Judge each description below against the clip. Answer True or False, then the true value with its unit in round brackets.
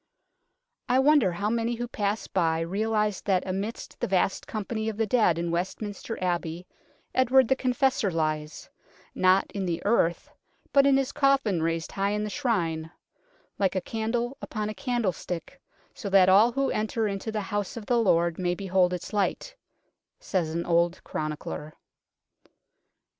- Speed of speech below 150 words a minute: False (165 wpm)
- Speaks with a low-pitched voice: False (205 Hz)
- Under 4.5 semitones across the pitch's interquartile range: False (4.9 semitones)